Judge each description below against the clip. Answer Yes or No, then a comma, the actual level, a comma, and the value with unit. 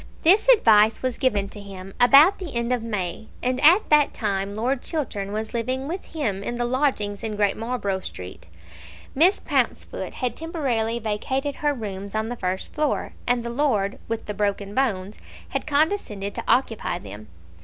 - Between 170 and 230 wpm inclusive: Yes, average, 175 wpm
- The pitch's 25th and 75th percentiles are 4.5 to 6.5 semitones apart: Yes, average, 5.1 semitones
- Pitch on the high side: Yes, high, 230 Hz